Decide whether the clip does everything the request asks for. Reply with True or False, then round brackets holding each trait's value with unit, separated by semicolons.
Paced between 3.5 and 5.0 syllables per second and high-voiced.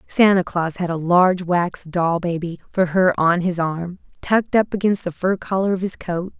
False (4.8 syllables/s; 180 Hz)